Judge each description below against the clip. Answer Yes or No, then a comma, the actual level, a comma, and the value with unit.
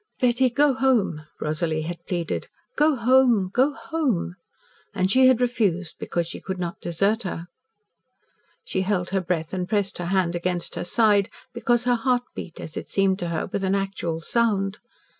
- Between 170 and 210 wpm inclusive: Yes, average, 175 wpm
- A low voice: No, high, 195 Hz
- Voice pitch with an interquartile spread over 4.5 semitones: Yes, wide, 5.5 semitones